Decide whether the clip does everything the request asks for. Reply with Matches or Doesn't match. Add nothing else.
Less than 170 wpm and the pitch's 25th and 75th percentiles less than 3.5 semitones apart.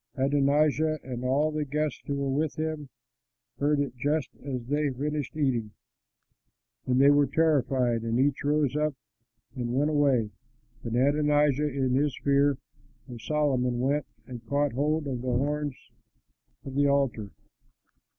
Matches